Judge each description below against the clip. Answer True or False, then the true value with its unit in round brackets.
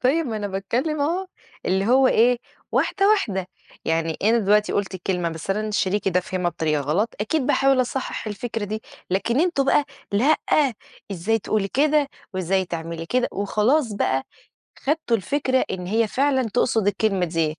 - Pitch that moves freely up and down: True (5.7 semitones)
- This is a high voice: True (215 Hz)